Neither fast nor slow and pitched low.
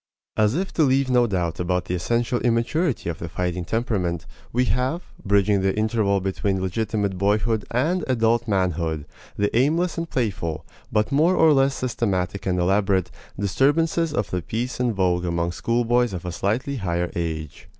Yes: average, 165 wpm; low, 105 Hz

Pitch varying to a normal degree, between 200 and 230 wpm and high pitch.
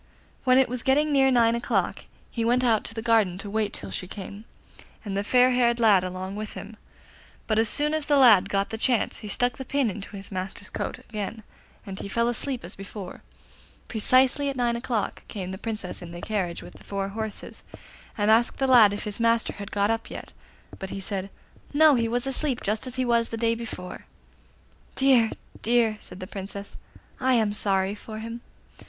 Yes: average, 3.6 semitones; fast, 205 wpm; high, 225 Hz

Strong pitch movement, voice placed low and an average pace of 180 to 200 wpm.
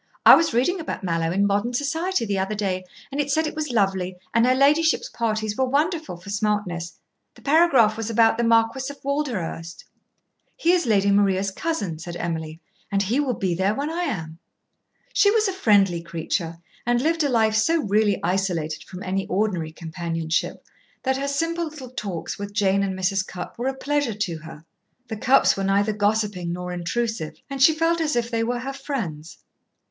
No: wide, 6.8 semitones; high, 215 Hz; average, 190 wpm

